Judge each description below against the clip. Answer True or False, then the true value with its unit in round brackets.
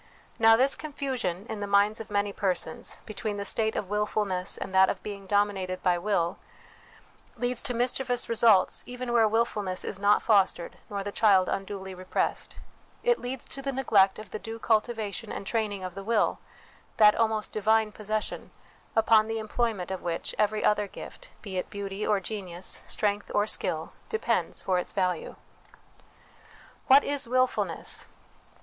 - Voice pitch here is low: False (210 Hz)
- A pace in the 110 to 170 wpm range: True (160 wpm)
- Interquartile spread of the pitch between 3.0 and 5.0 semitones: False (2.6 semitones)